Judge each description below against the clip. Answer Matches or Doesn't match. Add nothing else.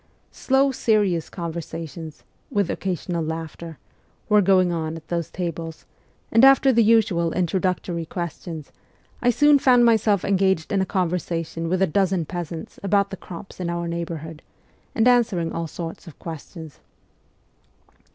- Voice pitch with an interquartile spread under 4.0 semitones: Matches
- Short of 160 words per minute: Matches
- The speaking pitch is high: Doesn't match